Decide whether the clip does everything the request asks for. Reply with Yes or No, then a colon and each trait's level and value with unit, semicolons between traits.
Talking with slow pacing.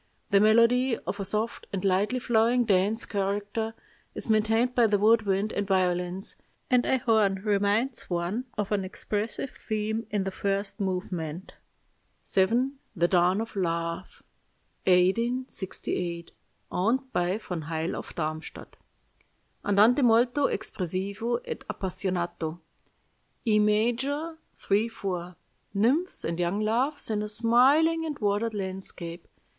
Yes: slow, 125 wpm